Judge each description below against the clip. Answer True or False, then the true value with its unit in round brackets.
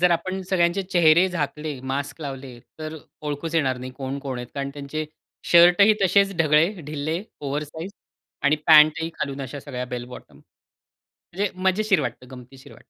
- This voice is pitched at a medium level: True (150 Hz)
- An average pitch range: True (3.9 semitones)